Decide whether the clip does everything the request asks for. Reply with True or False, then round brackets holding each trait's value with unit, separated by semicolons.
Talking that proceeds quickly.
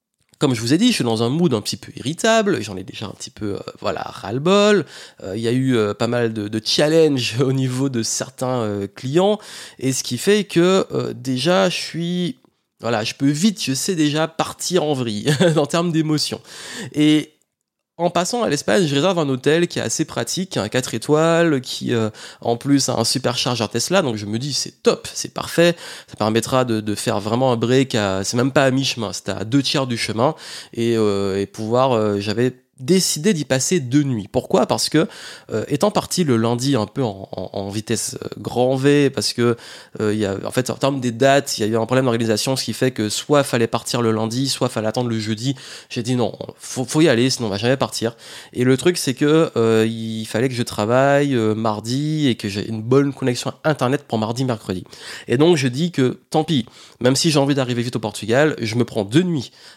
True (235 wpm)